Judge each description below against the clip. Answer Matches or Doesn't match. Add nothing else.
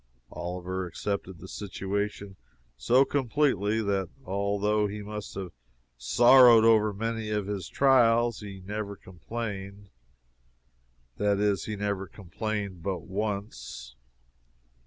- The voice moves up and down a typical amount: Doesn't match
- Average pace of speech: Doesn't match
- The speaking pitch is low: Matches